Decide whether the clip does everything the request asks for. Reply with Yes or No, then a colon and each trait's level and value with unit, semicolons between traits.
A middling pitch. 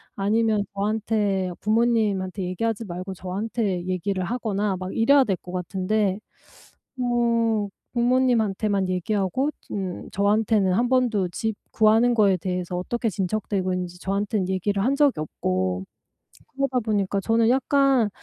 No: high, 205 Hz